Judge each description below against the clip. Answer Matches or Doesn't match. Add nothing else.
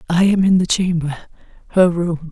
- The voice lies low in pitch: Doesn't match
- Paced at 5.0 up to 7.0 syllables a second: Matches